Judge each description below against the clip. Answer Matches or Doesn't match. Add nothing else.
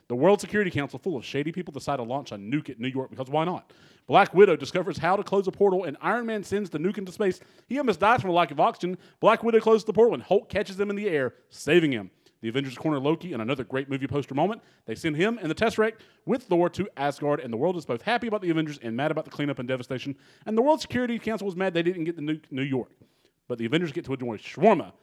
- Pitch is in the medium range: Matches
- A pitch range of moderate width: Doesn't match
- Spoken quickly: Matches